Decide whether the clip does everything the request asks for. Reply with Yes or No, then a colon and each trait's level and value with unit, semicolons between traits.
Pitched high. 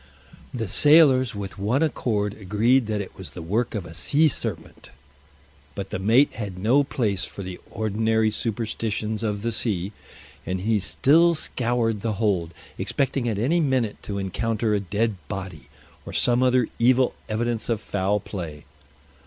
No: low, 110 Hz